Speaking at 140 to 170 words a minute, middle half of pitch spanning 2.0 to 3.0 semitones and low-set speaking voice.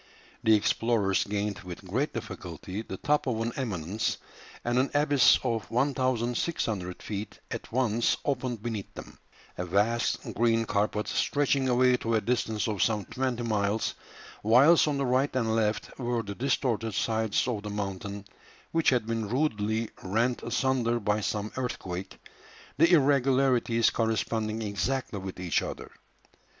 No: average, 145 wpm; average, 3.5 semitones; low, 115 Hz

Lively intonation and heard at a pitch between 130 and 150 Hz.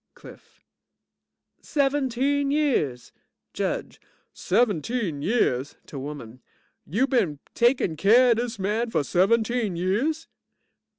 No: wide, 7.2 semitones; high, 230 Hz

